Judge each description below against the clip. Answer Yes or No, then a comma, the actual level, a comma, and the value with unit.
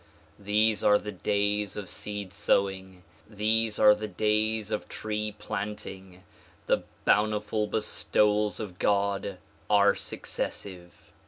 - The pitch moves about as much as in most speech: No, narrow, 1.3 semitones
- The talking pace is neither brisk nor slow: No, slow, 110 wpm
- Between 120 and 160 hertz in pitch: No, low, 105 Hz